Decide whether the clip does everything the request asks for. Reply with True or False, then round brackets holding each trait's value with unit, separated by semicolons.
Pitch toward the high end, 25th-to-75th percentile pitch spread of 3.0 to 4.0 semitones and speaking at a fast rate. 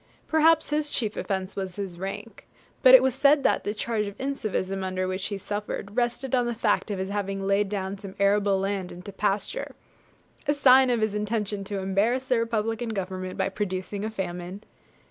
False (205 Hz; 3.3 semitones; 195 wpm)